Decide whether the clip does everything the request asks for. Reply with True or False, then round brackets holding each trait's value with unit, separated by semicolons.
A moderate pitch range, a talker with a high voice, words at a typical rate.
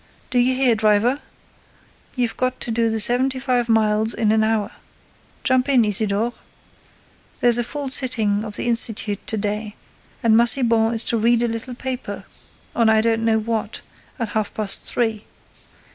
False (2.0 semitones; 230 Hz; 160 wpm)